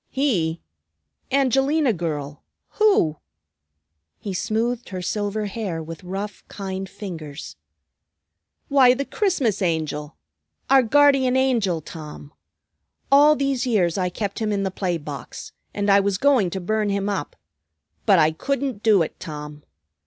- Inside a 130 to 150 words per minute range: Yes, slow, 135 wpm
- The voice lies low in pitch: No, high, 200 Hz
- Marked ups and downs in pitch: Yes, wide, 7.1 semitones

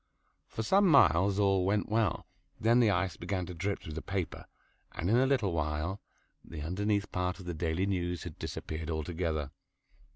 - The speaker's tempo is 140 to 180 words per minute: Yes, average, 175 wpm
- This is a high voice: No, very low, 90 Hz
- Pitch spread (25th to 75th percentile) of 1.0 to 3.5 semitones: No, average, 3.9 semitones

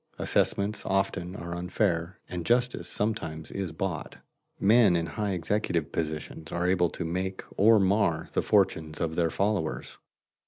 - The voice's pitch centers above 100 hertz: No, very low, 90 Hz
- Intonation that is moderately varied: Yes, average, 3.3 semitones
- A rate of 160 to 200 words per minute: No, average, 145 wpm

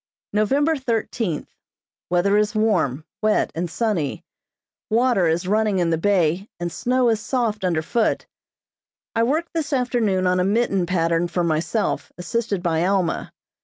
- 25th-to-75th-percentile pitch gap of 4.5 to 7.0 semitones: Yes, average, 4.9 semitones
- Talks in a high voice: Yes, high, 200 Hz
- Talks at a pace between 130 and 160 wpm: Yes, average, 145 wpm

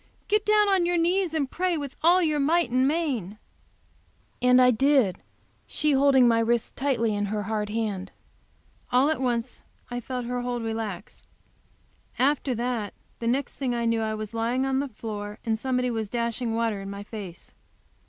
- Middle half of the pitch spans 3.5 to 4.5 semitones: Yes, average, 4.0 semitones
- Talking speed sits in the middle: Yes, average, 175 wpm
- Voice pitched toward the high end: Yes, high, 245 Hz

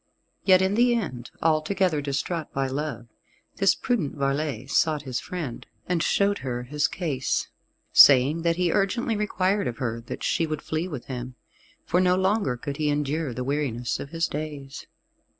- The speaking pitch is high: No, medium, 150 Hz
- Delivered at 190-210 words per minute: No, average, 170 wpm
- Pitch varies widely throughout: No, average, 5.0 semitones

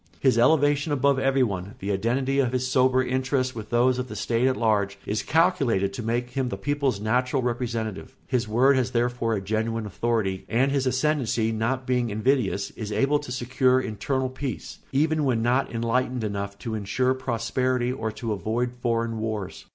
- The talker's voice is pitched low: Yes, low, 125 Hz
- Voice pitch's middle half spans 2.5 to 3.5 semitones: Yes, average, 2.9 semitones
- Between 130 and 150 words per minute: No, average, 175 wpm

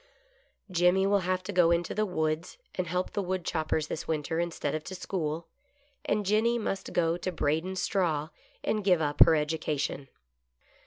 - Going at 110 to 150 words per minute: No, average, 170 wpm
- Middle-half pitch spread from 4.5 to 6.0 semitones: No, average, 3.1 semitones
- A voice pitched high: No, medium, 175 Hz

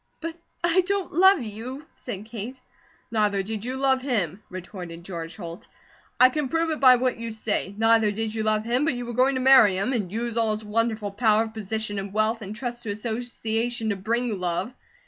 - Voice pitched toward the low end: No, high, 225 Hz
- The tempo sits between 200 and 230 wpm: Yes, fast, 205 wpm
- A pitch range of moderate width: Yes, average, 3.3 semitones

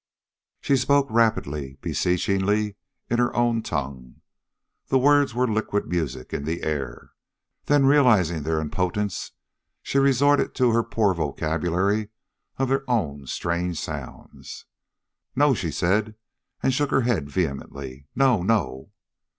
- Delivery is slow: Yes, slow, 125 wpm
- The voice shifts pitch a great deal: Yes, wide, 7.9 semitones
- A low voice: Yes, low, 100 Hz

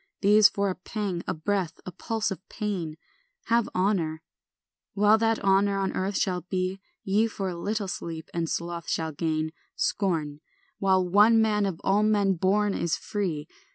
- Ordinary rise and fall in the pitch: Yes, average, 3.4 semitones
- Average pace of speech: Yes, average, 165 wpm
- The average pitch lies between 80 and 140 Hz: No, high, 195 Hz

